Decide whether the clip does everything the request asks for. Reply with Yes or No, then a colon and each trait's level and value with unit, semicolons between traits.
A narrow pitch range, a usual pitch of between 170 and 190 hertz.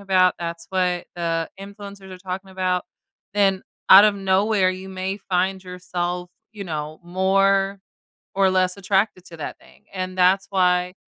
Yes: narrow, 1.3 semitones; medium, 185 Hz